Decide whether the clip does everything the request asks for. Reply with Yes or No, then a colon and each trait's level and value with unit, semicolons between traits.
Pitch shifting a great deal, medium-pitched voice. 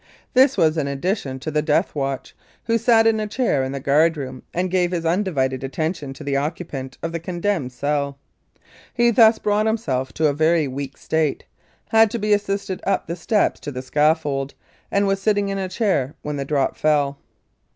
Yes: wide, 6.2 semitones; medium, 160 Hz